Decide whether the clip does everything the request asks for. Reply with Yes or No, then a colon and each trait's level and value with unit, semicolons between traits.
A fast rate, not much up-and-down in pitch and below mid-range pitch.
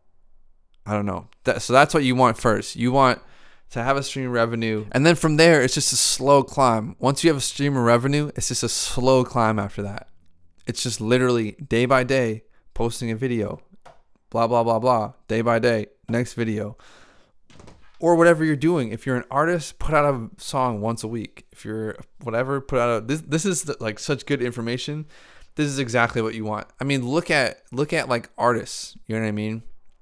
No: fast, 210 wpm; average, 3.9 semitones; low, 125 Hz